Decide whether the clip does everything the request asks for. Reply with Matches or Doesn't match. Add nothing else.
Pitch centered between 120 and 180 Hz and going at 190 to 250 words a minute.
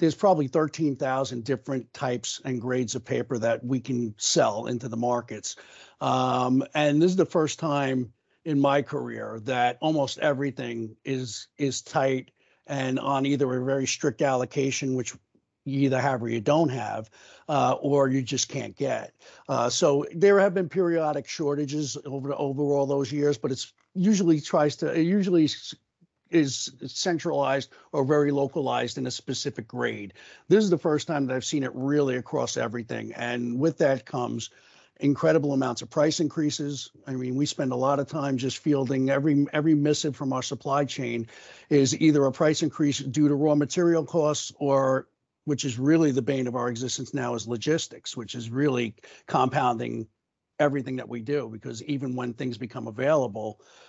Doesn't match